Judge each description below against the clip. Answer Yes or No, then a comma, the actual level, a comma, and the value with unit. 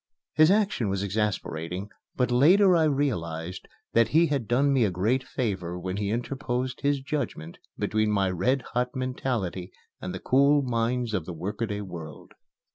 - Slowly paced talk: No, average, 160 wpm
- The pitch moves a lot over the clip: Yes, wide, 6.1 semitones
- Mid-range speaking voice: No, low, 115 Hz